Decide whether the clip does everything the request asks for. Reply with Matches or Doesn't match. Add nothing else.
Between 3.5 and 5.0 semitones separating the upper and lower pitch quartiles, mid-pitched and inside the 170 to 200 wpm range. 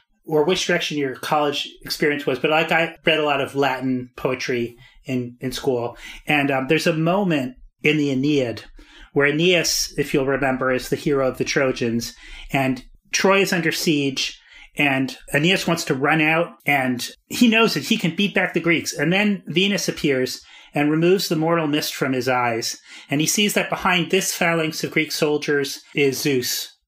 Matches